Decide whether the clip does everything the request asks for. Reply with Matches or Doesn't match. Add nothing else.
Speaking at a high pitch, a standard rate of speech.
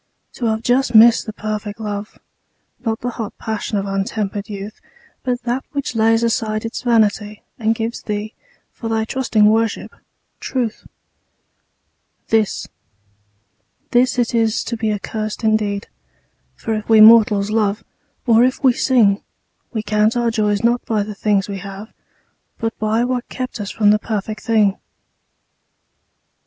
Matches